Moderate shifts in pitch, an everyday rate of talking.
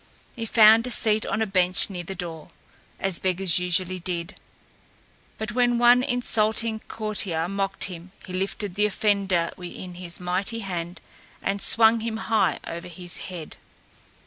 Yes: average, 3.6 semitones; average, 150 wpm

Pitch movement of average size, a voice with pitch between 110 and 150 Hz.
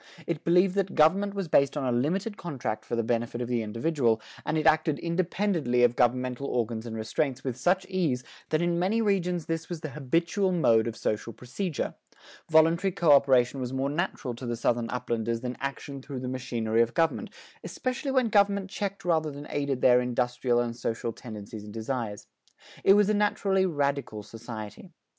No: wide, 6.4 semitones; medium, 140 Hz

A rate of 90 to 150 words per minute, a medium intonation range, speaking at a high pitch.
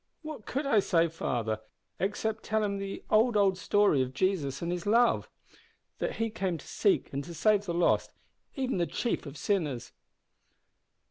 No: average, 175 wpm; average, 4.6 semitones; high, 195 Hz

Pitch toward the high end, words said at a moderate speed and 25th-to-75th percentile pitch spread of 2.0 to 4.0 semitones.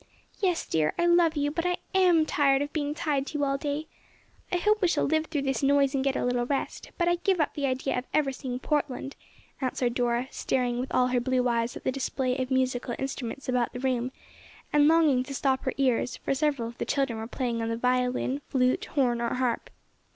No: very high, 270 Hz; fast, 225 wpm; average, 2.9 semitones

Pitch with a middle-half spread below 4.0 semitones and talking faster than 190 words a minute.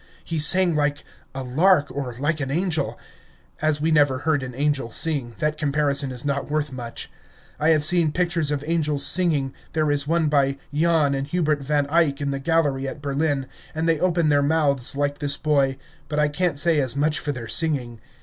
Yes: narrow, 2.4 semitones; average, 200 wpm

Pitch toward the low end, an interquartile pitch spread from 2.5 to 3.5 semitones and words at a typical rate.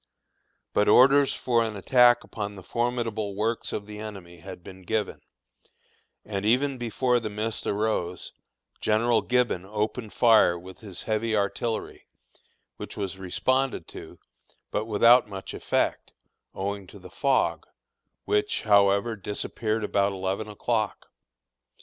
No: low, 105 Hz; average, 3.0 semitones; slow, 130 wpm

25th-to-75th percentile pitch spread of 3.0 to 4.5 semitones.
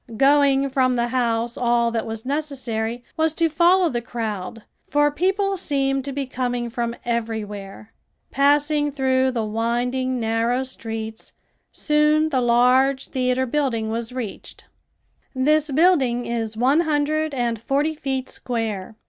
Yes: average, 3.8 semitones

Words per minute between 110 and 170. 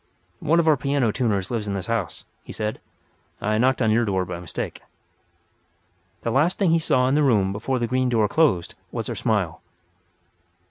No: average, 190 wpm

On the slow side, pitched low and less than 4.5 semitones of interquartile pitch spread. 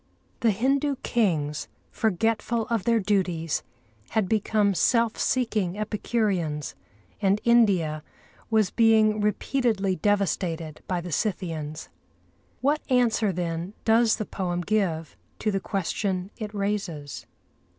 No: slow, 110 wpm; high, 205 Hz; average, 4.1 semitones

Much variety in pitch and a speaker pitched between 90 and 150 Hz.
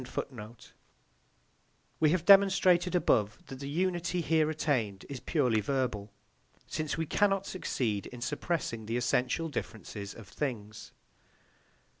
Yes: wide, 7.2 semitones; medium, 140 Hz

